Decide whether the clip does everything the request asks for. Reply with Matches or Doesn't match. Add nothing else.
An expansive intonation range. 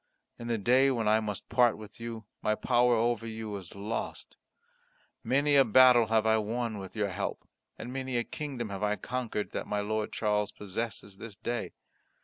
Doesn't match